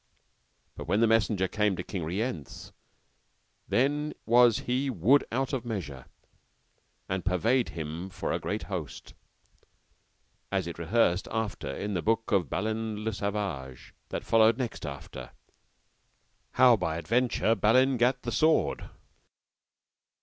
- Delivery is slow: Yes, slow, 130 wpm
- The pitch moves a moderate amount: Yes, average, 4.9 semitones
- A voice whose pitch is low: Yes, low, 110 Hz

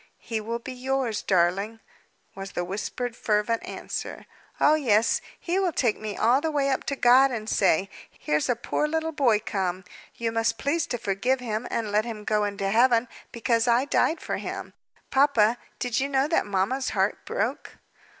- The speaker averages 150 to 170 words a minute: No, average, 180 wpm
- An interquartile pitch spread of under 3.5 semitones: No, average, 4.0 semitones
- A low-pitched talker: No, high, 230 Hz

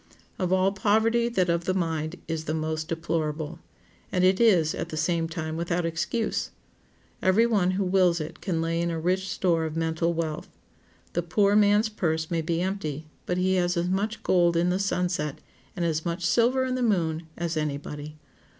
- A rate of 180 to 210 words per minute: Yes, average, 195 wpm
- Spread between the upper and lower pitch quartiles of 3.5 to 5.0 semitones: No, average, 2.8 semitones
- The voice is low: No, medium, 170 Hz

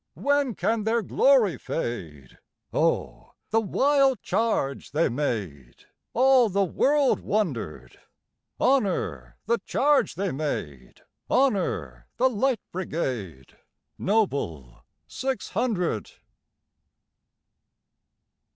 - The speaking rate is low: Yes, slow, 70 wpm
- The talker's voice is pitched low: No, high, 190 Hz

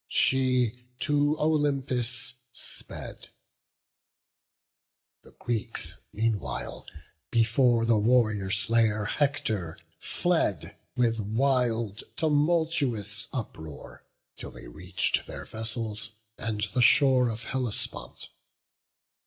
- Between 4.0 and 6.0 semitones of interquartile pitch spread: No, average, 3.6 semitones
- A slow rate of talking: Yes, slow, 85 wpm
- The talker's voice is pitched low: Yes, low, 115 Hz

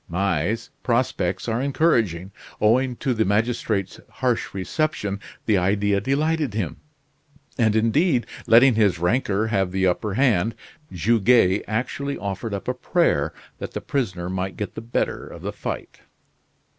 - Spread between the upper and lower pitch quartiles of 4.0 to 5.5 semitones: Yes, average, 4.5 semitones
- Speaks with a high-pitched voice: No, low, 110 Hz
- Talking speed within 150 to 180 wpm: No, average, 140 wpm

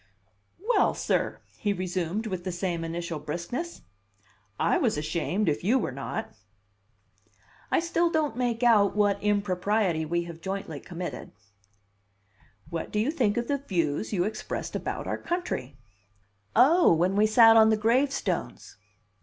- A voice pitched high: Yes, high, 200 Hz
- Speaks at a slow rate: No, average, 145 wpm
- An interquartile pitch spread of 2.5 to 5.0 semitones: No, wide, 5.4 semitones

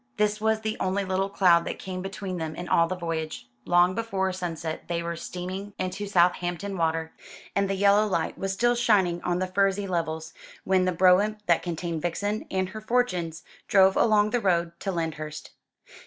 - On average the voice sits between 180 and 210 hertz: Yes, medium, 185 Hz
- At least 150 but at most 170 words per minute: No, average, 185 wpm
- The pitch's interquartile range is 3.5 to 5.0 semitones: No, average, 2.9 semitones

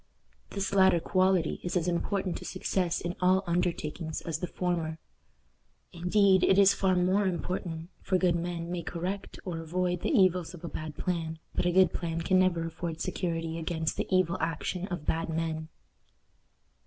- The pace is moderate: Yes, average, 170 wpm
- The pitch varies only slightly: Yes, narrow, 2.1 semitones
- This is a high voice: No, medium, 175 Hz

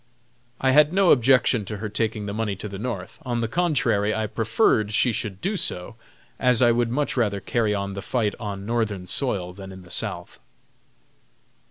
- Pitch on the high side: No, low, 110 Hz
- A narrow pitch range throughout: No, average, 3.5 semitones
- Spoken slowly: No, average, 190 wpm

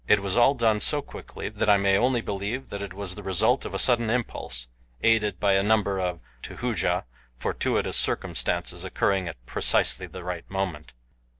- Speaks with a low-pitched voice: Yes, low, 100 Hz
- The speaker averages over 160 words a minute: Yes, average, 180 wpm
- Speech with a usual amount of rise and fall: Yes, average, 3.2 semitones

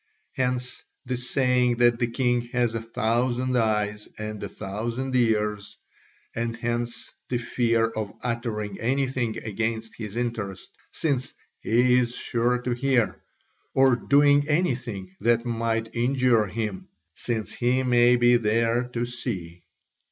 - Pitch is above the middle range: No, low, 120 Hz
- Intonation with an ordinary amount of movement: No, narrow, 1.9 semitones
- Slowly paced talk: Yes, slow, 130 wpm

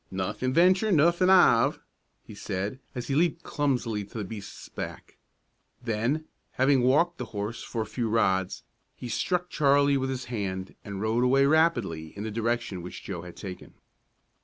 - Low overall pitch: Yes, low, 120 Hz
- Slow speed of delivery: No, average, 165 wpm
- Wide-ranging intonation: Yes, wide, 5.8 semitones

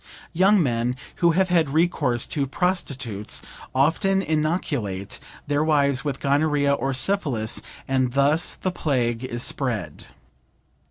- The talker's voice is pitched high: No, medium, 140 Hz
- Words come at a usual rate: No, slow, 120 wpm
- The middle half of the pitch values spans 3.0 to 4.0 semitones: No, average, 4.6 semitones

